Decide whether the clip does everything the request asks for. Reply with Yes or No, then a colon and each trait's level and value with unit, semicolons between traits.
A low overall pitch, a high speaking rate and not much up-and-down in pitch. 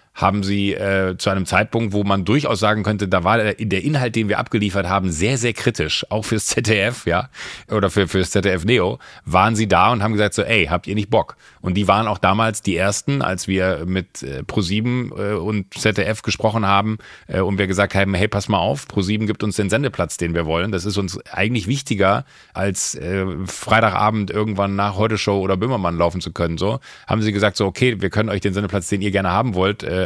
Yes: low, 100 Hz; fast, 225 wpm; narrow, 2.1 semitones